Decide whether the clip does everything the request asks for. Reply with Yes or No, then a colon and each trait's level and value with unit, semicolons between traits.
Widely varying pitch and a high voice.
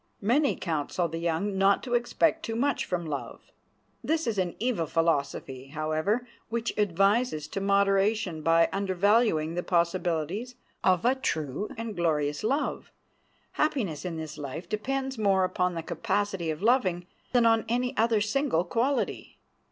Yes: wide, 5.7 semitones; high, 195 Hz